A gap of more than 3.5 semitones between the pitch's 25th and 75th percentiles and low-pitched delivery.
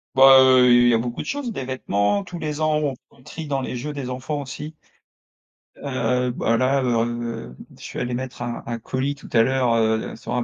No: average, 2.9 semitones; low, 130 Hz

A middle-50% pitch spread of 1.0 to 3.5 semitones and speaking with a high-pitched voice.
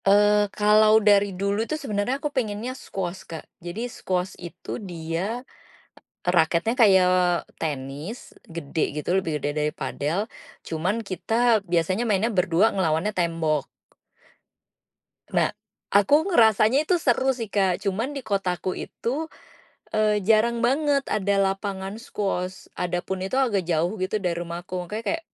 No: average, 4.0 semitones; high, 195 Hz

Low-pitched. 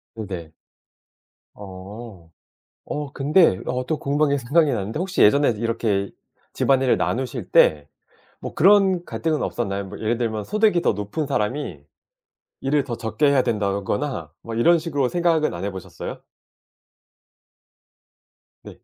Yes: low, 125 Hz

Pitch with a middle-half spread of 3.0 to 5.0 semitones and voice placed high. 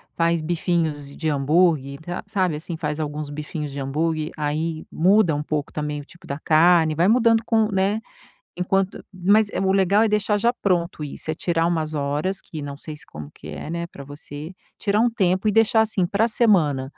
No: average, 4.5 semitones; medium, 165 Hz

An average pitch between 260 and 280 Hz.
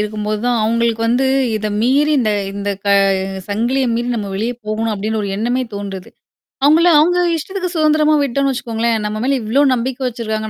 No: high, 235 Hz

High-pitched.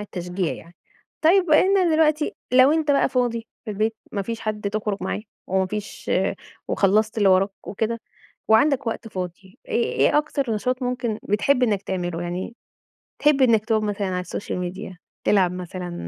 Yes: high, 215 Hz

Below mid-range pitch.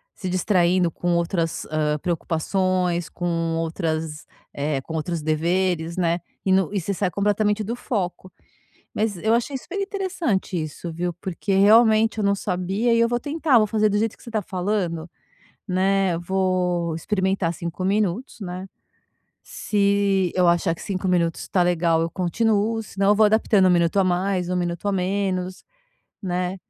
No: medium, 185 Hz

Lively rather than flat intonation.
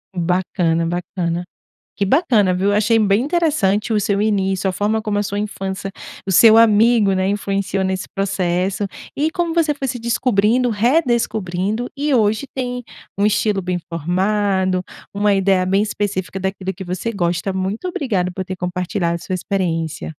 No: average, 3.0 semitones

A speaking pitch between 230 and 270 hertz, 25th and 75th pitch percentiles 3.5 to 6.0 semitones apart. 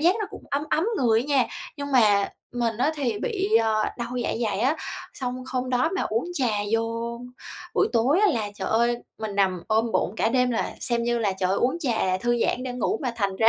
No: high, 240 Hz; average, 2.9 semitones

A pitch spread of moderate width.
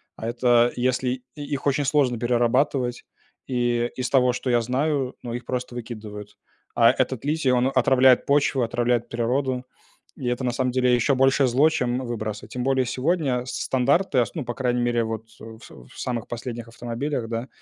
No: narrow, 1.8 semitones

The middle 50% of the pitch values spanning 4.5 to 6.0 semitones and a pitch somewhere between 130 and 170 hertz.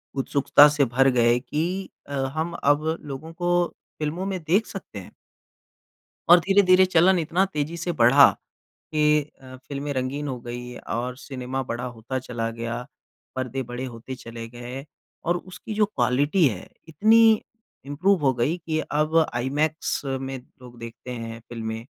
Yes: average, 5.1 semitones; medium, 140 Hz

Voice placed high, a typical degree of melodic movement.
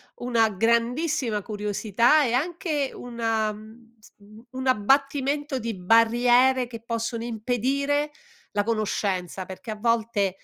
Yes: high, 235 Hz; average, 3.3 semitones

